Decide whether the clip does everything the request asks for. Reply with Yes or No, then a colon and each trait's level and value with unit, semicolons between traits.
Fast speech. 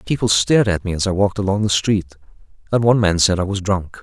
Yes: fast, 255 wpm